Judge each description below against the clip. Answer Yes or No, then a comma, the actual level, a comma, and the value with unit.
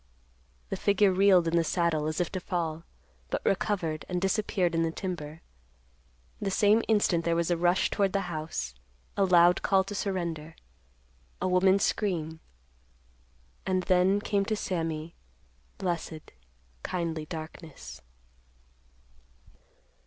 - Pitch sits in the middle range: Yes, medium, 170 Hz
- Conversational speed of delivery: No, slow, 125 wpm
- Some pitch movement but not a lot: Yes, average, 3.5 semitones